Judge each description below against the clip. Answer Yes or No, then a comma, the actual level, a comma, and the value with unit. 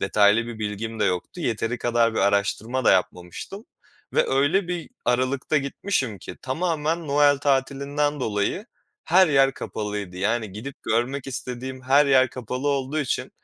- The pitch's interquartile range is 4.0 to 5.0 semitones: Yes, average, 4.3 semitones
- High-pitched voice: No, low, 130 Hz